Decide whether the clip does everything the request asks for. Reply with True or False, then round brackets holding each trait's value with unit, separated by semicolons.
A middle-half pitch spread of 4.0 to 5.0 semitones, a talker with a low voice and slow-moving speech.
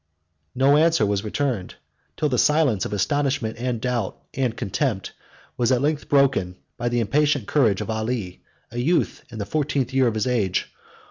False (4.5 semitones; 125 Hz; 180 wpm)